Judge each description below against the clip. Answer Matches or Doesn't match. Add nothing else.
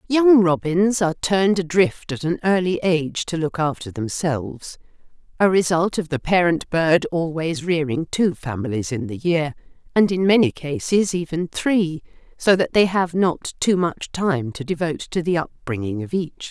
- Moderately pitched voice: Matches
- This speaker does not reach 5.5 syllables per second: Matches